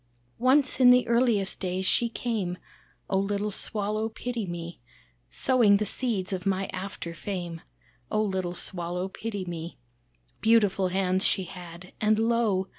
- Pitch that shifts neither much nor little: Yes, average, 3.5 semitones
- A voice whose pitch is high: Yes, high, 195 Hz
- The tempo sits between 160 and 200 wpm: No, average, 140 wpm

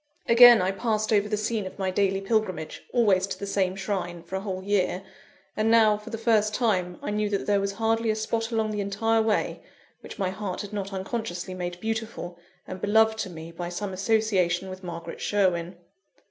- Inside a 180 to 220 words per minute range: Yes, average, 200 wpm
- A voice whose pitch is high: Yes, high, 200 Hz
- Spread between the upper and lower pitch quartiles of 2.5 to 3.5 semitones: Yes, average, 2.8 semitones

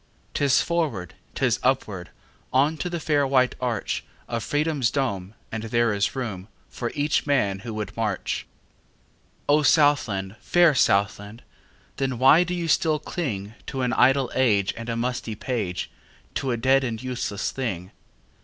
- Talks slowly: Yes, slow, 130 wpm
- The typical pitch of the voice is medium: No, low, 125 Hz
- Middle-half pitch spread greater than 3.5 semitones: Yes, average, 5.1 semitones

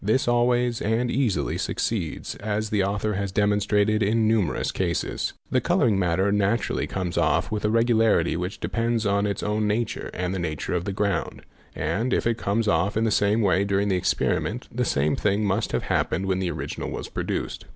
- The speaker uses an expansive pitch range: No, average, 2.7 semitones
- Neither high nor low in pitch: No, low, 105 Hz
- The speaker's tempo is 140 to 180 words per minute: No, average, 200 wpm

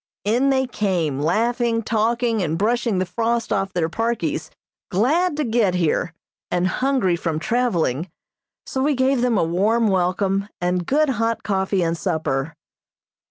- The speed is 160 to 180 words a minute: No, average, 150 wpm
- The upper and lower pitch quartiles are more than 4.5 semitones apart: Yes, average, 5.1 semitones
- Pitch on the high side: Yes, high, 210 Hz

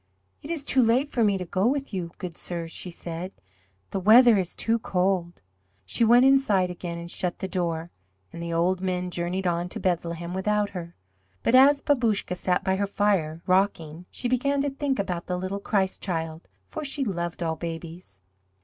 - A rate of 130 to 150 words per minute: No, average, 190 wpm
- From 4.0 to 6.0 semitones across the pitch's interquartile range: Yes, average, 4.6 semitones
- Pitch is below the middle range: No, medium, 185 Hz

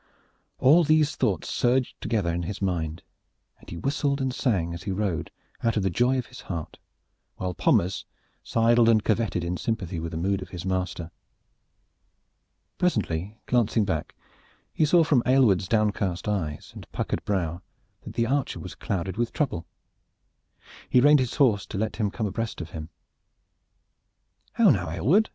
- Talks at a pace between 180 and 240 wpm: No, average, 165 wpm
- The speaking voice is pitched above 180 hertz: No, low, 105 Hz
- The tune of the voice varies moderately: No, wide, 5.8 semitones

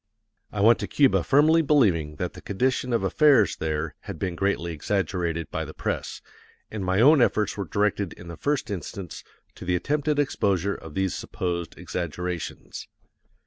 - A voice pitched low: Yes, very low, 95 Hz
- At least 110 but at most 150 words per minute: No, average, 165 wpm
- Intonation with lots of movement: Yes, wide, 6.2 semitones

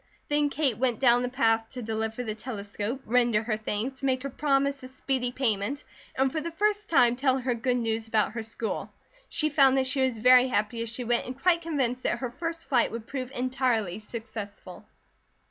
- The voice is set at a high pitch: Yes, very high, 250 Hz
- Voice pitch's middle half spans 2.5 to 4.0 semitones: Yes, average, 3.2 semitones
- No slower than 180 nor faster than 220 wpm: Yes, average, 200 wpm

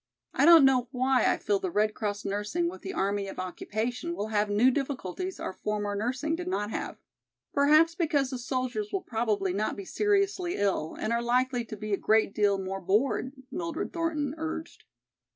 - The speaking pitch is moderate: No, very high, 250 Hz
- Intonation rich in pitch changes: Yes, wide, 7.6 semitones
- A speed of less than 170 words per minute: No, average, 190 wpm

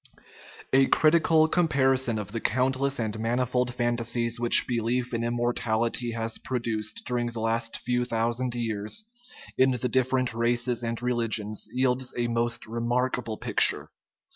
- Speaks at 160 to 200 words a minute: No, slow, 135 wpm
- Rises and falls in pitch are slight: Yes, narrow, 1.7 semitones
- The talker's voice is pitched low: Yes, low, 120 Hz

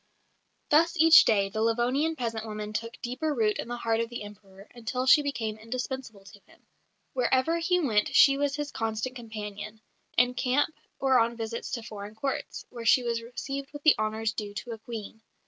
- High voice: Yes, high, 235 Hz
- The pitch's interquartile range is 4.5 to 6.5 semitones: No, average, 3.5 semitones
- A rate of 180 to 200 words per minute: Yes, average, 190 wpm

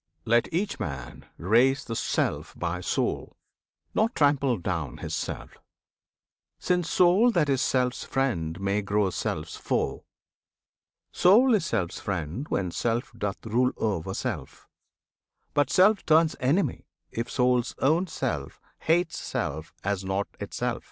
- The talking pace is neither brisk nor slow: No, slow, 130 wpm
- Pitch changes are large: Yes, wide, 8.4 semitones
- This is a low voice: Yes, low, 125 Hz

